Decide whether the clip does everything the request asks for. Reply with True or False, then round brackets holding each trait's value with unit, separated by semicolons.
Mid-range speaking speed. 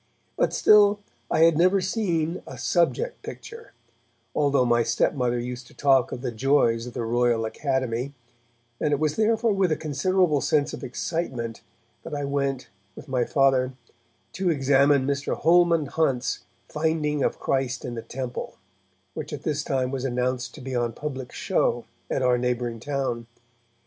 True (160 wpm)